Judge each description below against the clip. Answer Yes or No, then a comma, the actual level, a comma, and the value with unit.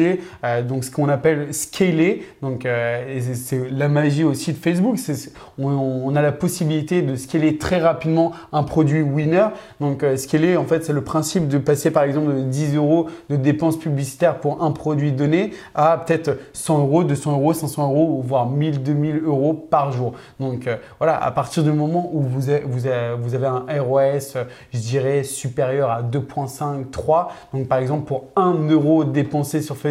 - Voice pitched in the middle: Yes, medium, 145 Hz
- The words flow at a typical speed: Yes, average, 175 wpm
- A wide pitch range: No, average, 2.7 semitones